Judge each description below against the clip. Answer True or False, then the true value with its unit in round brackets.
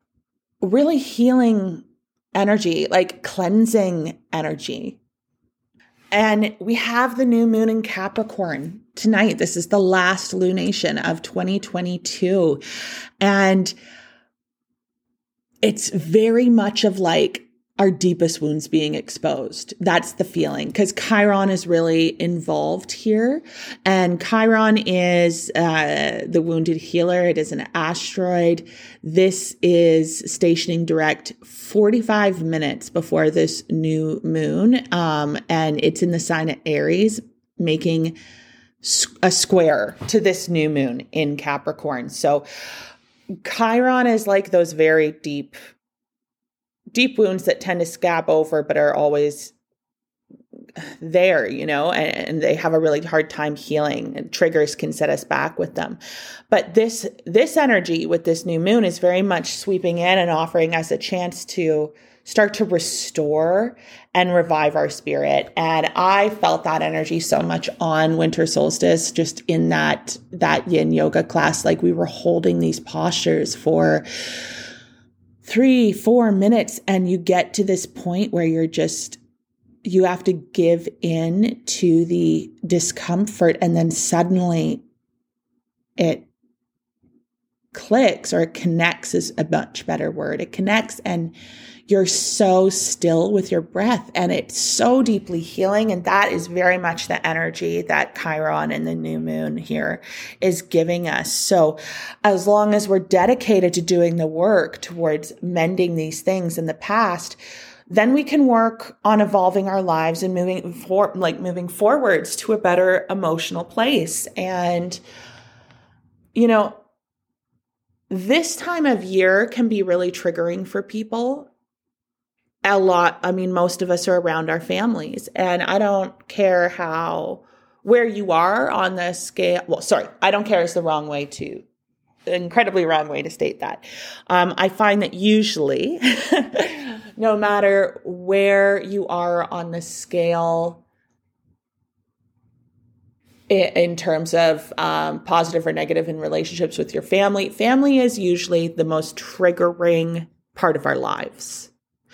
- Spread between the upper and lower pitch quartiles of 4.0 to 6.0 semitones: True (4.5 semitones)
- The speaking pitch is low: False (180 Hz)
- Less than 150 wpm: True (140 wpm)